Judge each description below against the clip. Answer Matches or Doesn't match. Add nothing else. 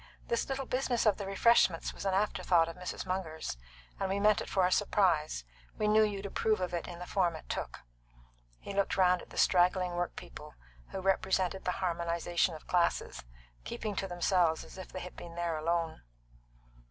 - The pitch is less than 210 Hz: Matches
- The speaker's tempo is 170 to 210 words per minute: Matches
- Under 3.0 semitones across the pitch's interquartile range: Matches